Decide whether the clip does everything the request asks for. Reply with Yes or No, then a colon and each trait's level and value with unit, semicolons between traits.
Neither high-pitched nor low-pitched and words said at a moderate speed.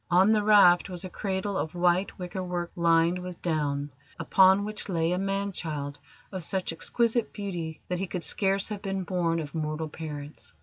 Yes: medium, 180 Hz; average, 185 wpm